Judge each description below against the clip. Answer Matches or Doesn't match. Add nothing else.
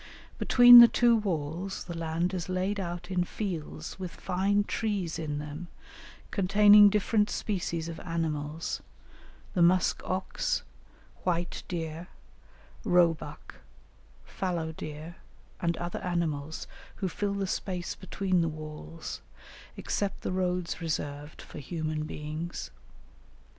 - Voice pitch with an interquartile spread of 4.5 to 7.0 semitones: Doesn't match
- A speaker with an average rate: Doesn't match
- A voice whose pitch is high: Doesn't match